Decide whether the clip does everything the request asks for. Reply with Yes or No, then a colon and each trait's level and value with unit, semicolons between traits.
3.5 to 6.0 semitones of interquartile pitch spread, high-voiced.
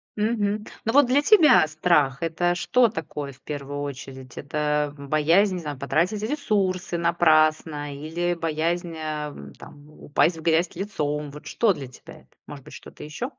No: average, 3.9 semitones; medium, 160 Hz